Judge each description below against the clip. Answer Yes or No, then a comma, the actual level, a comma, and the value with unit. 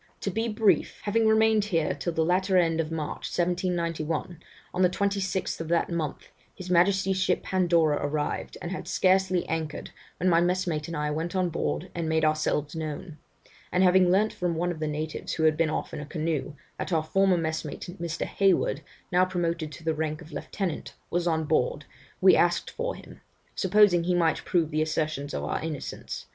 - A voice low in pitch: No, medium, 170 Hz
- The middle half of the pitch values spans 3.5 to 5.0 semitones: No, average, 2.9 semitones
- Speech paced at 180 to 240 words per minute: Yes, average, 190 wpm